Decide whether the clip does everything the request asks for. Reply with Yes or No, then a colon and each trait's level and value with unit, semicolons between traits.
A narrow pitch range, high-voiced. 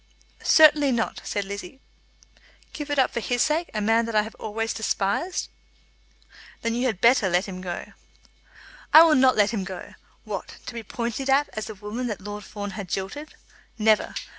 No: average, 4.2 semitones; high, 225 Hz